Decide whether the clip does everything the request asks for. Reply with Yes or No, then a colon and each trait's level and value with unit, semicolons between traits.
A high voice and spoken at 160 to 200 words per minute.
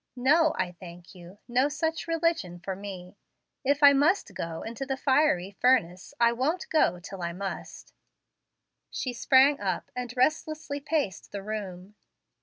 No: high, 245 Hz; average, 150 wpm